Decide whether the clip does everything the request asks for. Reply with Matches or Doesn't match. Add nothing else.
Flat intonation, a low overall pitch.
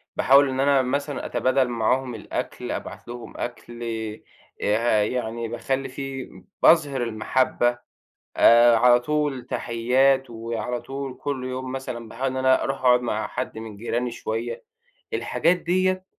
Matches